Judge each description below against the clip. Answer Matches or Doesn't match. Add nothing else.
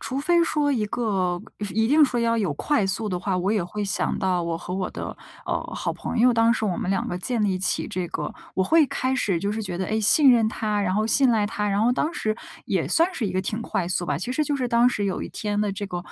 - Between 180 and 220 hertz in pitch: Matches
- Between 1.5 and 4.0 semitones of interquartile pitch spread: Doesn't match